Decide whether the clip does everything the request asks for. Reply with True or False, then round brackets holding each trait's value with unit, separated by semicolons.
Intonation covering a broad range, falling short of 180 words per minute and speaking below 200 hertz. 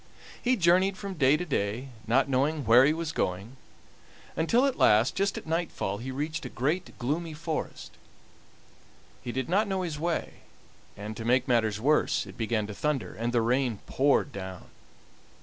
True (6.1 semitones; 170 wpm; 135 Hz)